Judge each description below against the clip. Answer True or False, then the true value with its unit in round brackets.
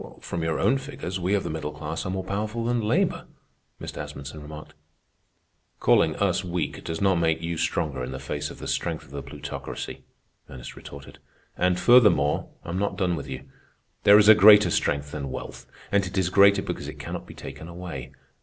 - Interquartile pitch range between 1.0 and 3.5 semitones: False (5.1 semitones)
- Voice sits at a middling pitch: False (85 Hz)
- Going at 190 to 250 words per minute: True (195 wpm)